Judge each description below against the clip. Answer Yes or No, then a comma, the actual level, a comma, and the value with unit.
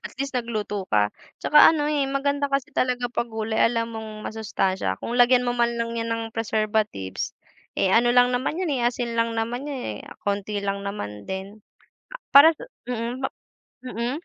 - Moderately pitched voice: No, high, 230 Hz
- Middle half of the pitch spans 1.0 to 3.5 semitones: Yes, average, 3.1 semitones